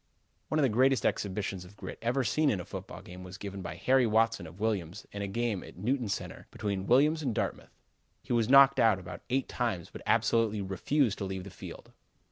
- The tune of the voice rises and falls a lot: No, average, 4.7 semitones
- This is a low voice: Yes, low, 110 Hz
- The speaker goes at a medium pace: No, fast, 215 wpm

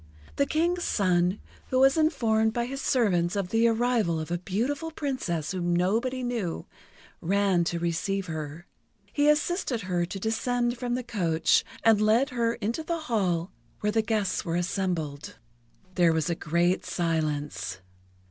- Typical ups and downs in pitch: No, wide, 6.0 semitones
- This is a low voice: No, high, 205 Hz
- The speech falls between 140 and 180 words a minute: Yes, average, 155 wpm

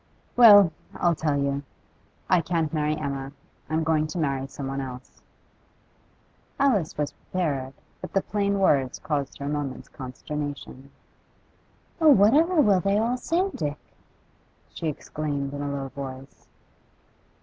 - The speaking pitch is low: No, medium, 150 Hz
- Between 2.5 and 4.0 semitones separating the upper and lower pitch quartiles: No, average, 5.3 semitones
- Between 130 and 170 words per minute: Yes, average, 140 wpm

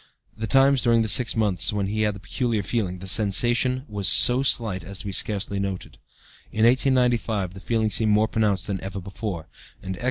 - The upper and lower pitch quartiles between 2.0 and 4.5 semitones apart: Yes, average, 3.3 semitones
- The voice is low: Yes, low, 105 Hz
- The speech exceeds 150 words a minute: Yes, average, 200 wpm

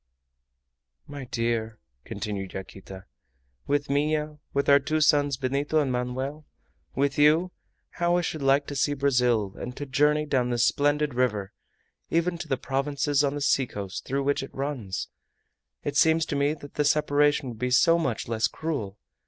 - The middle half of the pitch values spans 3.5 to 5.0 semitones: No, average, 3.1 semitones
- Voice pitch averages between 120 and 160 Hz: Yes, medium, 140 Hz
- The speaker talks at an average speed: Yes, average, 165 wpm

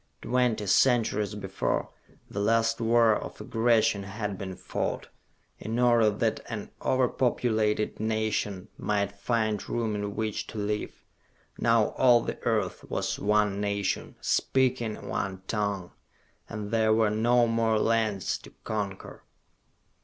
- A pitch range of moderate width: No, narrow, 2.0 semitones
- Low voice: Yes, low, 110 Hz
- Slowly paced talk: Yes, slow, 130 wpm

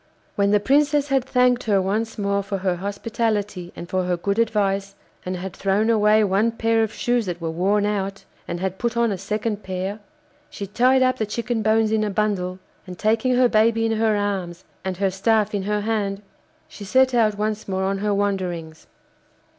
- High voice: Yes, high, 205 Hz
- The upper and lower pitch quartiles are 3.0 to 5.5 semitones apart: No, narrow, 2.6 semitones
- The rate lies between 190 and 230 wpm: Yes, average, 200 wpm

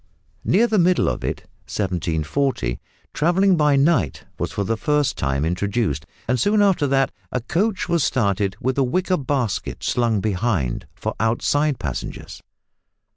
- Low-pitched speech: Yes, low, 130 Hz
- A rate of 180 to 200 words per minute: No, average, 145 wpm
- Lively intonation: Yes, wide, 7.6 semitones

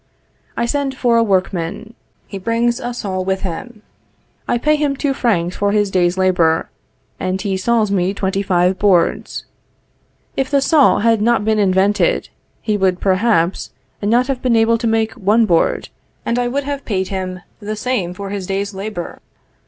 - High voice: Yes, high, 205 Hz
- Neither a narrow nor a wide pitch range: Yes, average, 3.9 semitones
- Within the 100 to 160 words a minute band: No, average, 175 wpm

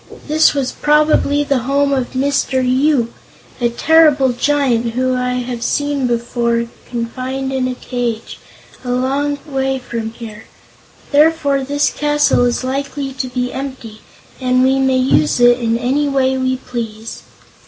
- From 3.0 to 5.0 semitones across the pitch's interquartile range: No, narrow, 2.5 semitones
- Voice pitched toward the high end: Yes, very high, 260 Hz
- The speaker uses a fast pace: No, average, 145 wpm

